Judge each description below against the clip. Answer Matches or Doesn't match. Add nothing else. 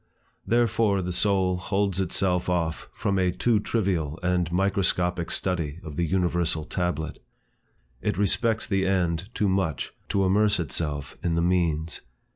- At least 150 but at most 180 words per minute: Doesn't match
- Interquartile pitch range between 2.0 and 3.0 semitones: Matches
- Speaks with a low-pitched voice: Matches